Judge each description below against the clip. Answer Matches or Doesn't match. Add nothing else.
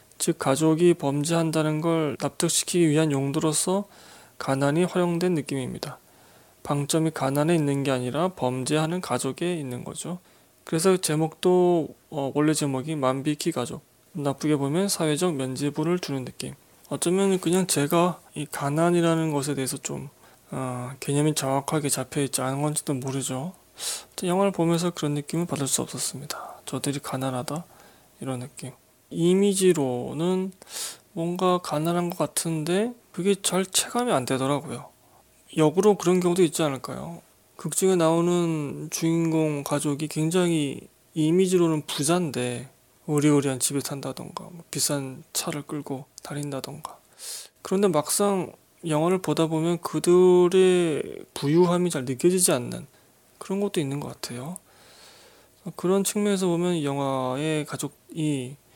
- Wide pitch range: Doesn't match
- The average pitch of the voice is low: Doesn't match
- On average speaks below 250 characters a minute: Doesn't match